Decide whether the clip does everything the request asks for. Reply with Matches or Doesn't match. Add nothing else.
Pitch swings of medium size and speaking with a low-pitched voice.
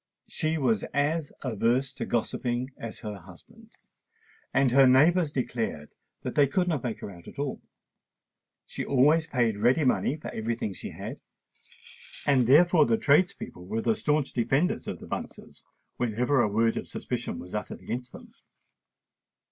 Matches